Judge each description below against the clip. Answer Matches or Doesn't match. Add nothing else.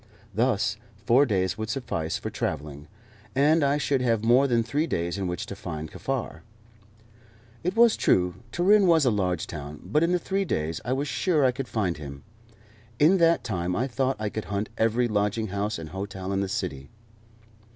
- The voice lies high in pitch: Doesn't match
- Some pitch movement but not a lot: Doesn't match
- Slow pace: Doesn't match